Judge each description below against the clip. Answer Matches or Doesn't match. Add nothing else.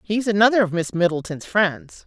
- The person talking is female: Matches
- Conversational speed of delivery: Matches